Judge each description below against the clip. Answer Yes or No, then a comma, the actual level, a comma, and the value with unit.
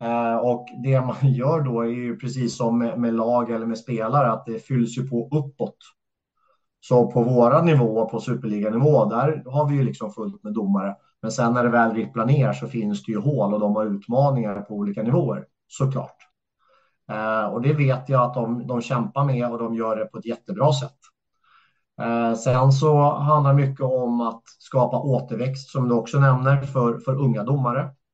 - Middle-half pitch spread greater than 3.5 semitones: No, average, 2.8 semitones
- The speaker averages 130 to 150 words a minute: No, fast, 195 wpm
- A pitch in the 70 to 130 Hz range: Yes, low, 120 Hz